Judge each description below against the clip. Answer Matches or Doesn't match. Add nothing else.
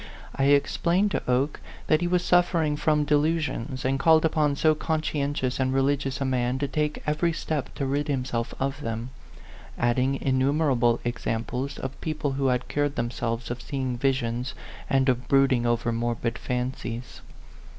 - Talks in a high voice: Doesn't match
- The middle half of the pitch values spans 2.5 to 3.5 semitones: Matches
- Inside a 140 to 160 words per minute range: Matches